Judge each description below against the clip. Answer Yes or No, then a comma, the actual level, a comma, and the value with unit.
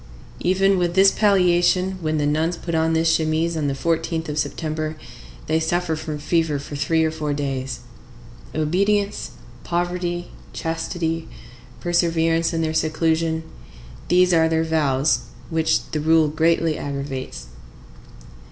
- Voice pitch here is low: No, medium, 160 Hz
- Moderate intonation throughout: No, narrow, 2.1 semitones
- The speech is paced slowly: Yes, slow, 130 wpm